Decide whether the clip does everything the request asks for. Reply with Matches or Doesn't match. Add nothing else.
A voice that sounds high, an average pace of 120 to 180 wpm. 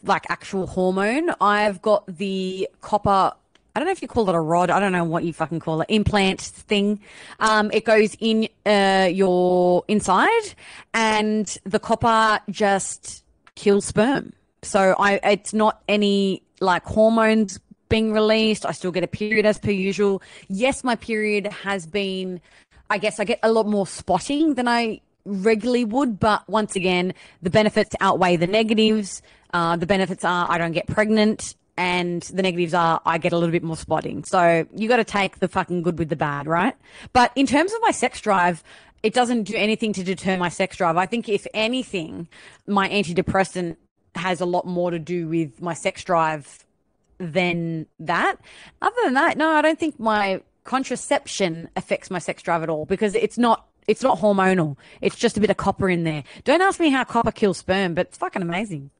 Doesn't match